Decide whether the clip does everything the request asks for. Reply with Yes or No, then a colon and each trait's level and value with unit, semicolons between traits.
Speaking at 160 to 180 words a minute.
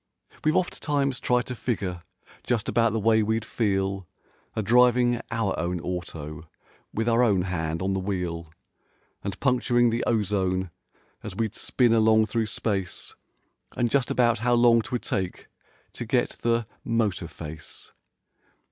No: average, 145 wpm